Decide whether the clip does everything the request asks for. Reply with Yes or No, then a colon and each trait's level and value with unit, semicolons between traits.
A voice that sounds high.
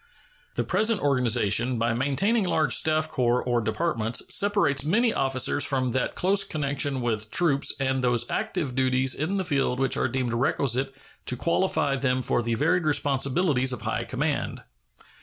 No: low, 135 Hz